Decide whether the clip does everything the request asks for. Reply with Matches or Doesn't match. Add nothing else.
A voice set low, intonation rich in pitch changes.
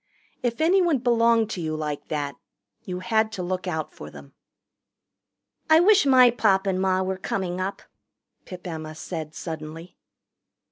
Doesn't match